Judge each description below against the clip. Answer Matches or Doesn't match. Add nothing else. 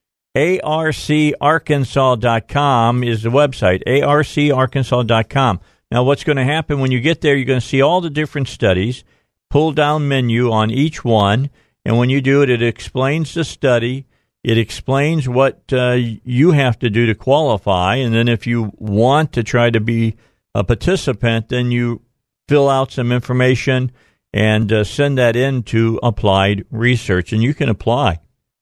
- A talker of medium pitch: Doesn't match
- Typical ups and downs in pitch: Matches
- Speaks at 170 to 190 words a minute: Doesn't match